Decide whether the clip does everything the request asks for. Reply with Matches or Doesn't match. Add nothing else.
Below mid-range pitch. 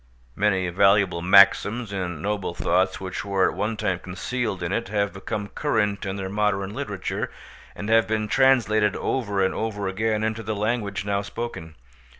Matches